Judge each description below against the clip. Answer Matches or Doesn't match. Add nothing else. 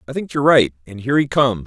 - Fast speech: Matches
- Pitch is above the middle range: Doesn't match